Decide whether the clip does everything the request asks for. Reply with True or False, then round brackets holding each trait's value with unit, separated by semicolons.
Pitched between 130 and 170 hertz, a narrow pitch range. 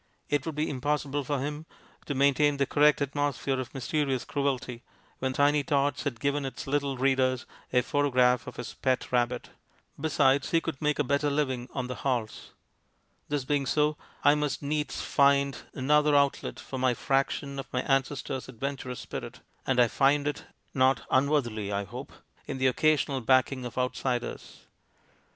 True (135 Hz; 2.1 semitones)